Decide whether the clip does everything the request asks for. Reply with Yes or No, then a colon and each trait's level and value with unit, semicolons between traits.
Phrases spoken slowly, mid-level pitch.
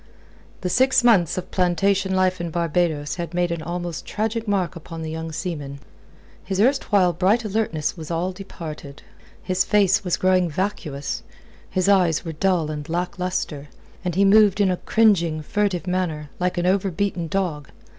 No: average, 165 wpm; medium, 180 Hz